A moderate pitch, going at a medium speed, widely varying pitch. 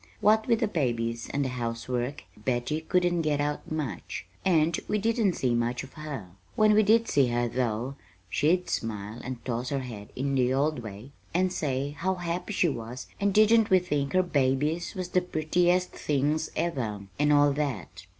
Yes: medium, 145 Hz; average, 180 wpm; wide, 6.3 semitones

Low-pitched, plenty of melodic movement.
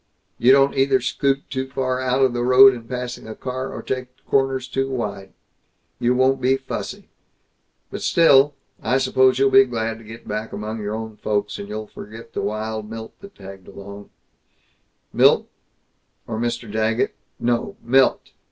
No: low, 120 Hz; average, 3.2 semitones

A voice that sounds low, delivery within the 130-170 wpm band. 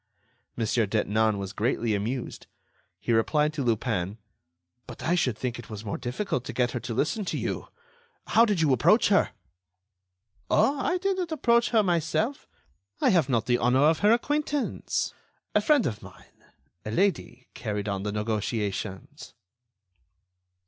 Yes: low, 125 Hz; average, 155 wpm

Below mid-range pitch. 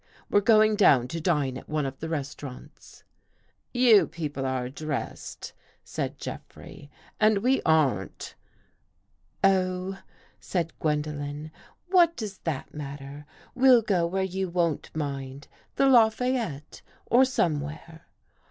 No: medium, 160 Hz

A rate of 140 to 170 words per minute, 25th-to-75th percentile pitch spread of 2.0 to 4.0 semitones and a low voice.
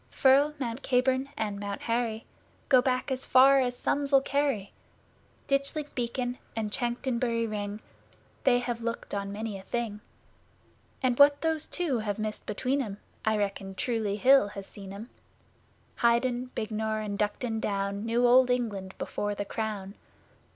No: average, 150 wpm; average, 3.7 semitones; high, 235 Hz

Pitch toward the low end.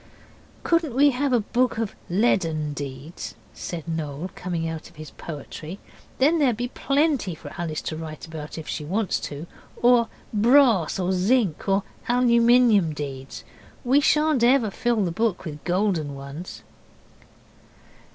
No: high, 190 Hz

